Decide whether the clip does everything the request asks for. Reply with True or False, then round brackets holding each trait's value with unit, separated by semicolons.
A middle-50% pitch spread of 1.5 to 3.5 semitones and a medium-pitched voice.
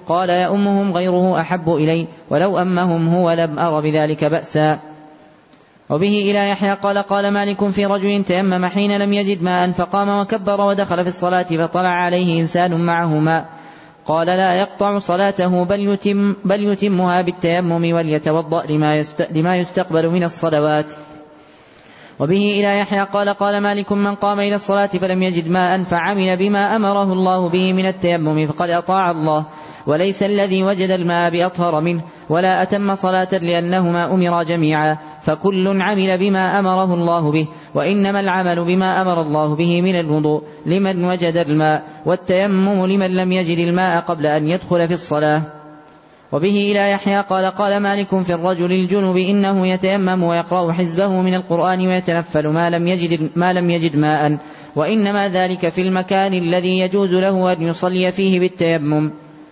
True (2.8 semitones; 180 Hz)